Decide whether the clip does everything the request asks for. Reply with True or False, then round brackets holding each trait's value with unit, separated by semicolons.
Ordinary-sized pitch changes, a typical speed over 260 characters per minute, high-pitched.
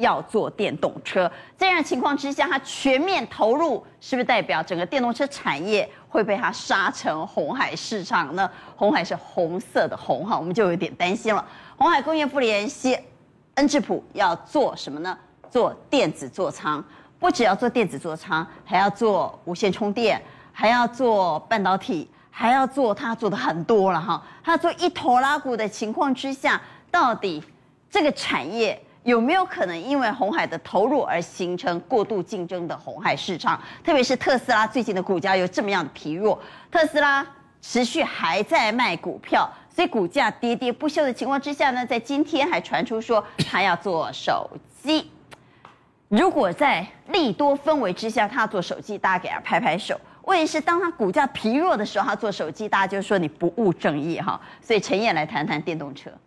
False (6.6 semitones; 275 characters per minute; 240 Hz)